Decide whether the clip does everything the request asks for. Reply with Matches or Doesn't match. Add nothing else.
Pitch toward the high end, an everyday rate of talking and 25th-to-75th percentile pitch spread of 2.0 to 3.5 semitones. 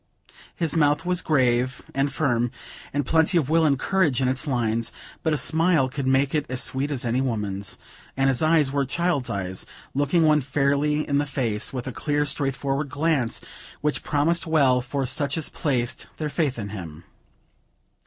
Doesn't match